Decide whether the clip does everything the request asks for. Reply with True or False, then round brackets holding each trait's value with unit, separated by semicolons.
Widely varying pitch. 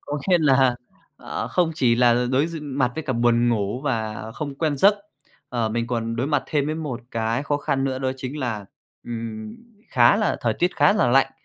False (3.7 semitones)